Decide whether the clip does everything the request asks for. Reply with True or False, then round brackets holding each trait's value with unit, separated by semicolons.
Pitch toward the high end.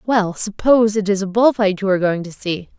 True (200 Hz)